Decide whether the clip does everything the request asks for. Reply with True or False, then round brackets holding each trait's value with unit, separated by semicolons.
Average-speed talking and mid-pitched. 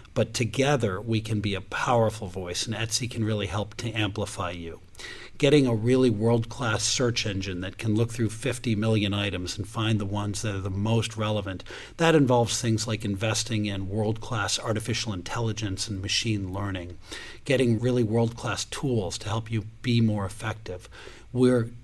False (175 wpm; 110 Hz)